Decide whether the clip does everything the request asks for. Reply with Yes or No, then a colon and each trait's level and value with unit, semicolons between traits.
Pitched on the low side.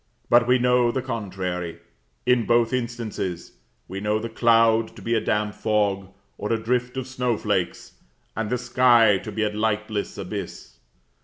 Yes: low, 115 Hz